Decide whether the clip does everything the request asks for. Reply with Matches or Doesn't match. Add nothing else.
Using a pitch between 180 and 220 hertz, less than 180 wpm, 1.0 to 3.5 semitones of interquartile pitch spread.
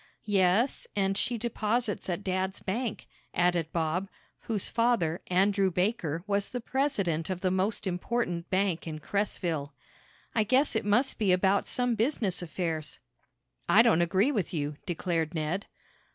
Doesn't match